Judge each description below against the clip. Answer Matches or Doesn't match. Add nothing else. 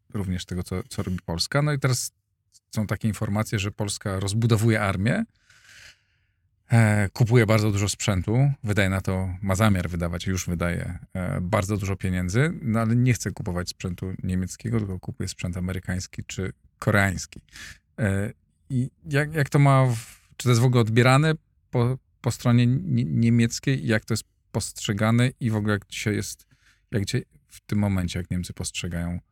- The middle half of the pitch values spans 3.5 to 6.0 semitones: Matches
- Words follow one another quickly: Matches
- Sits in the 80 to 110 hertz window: Matches